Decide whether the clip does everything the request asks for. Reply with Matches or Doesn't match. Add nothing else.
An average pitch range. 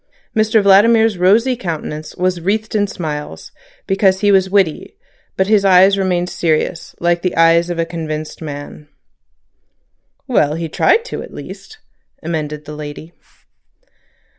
Matches